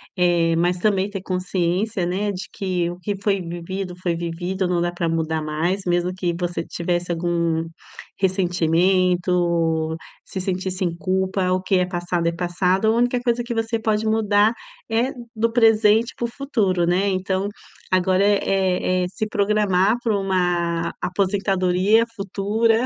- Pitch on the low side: No, medium, 185 Hz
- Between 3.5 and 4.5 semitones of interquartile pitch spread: No, average, 2.7 semitones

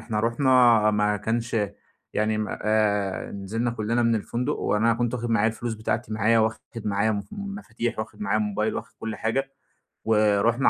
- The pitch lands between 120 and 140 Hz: No, low, 110 Hz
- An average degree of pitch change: No, narrow, 1.7 semitones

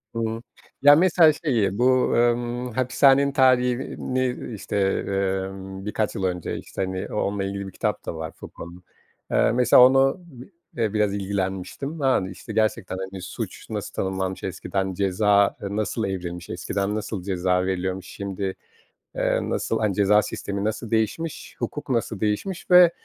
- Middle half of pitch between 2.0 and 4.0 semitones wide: No, average, 4.5 semitones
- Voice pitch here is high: No, low, 105 Hz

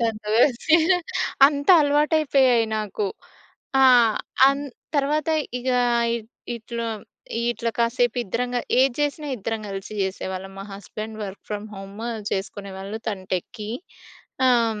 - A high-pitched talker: Yes, high, 225 Hz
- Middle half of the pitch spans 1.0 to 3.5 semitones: No, average, 4.5 semitones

